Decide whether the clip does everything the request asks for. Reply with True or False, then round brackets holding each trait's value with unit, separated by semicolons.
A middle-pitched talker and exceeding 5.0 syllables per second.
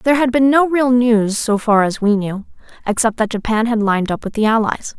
False (225 Hz; 5.5 syllables/s)